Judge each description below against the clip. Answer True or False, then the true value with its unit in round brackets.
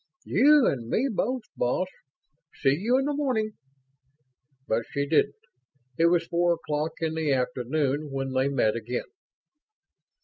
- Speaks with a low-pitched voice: False (155 Hz)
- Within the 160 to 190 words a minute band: False (140 wpm)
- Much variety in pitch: True (8.2 semitones)